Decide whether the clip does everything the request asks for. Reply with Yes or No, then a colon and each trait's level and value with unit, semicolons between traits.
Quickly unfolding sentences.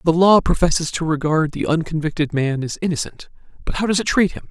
Yes: fast, 215 wpm